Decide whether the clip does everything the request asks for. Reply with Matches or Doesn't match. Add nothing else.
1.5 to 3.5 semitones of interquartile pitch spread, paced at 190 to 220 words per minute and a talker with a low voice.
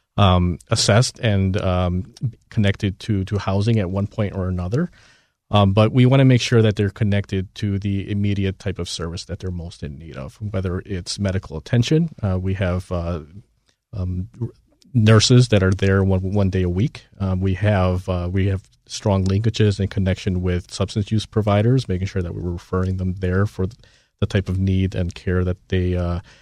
Matches